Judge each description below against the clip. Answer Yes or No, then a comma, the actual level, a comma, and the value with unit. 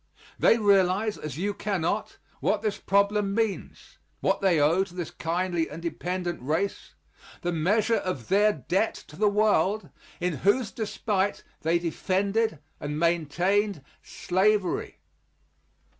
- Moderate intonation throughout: Yes, average, 3.5 semitones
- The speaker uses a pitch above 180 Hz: Yes, high, 190 Hz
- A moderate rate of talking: No, slow, 130 wpm